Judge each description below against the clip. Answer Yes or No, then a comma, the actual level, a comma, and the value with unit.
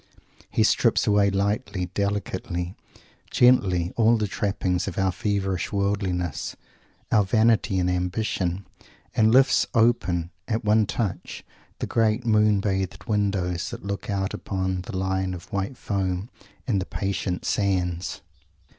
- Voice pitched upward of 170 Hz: No, low, 100 Hz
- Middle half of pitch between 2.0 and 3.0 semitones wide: Yes, narrow, 2.5 semitones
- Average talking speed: No, slow, 130 wpm